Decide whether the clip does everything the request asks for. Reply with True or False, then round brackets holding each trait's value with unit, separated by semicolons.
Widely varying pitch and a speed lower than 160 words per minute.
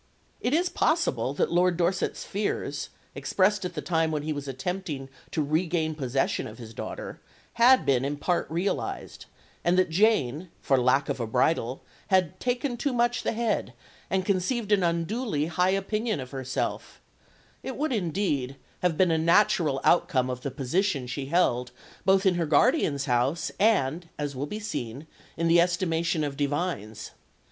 False (5.7 semitones; 165 wpm)